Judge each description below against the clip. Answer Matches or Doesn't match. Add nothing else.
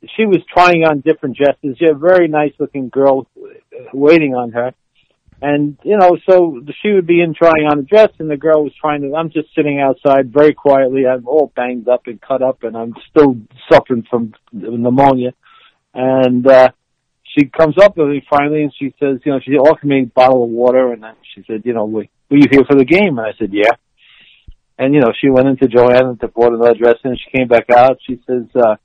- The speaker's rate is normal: Doesn't match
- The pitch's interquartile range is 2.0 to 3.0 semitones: Doesn't match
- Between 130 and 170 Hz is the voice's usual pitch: Matches